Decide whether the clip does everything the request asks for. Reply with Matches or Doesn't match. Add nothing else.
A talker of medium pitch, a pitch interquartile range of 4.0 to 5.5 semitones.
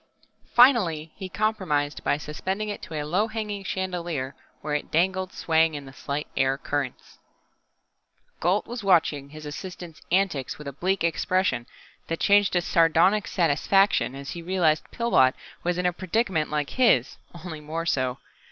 Matches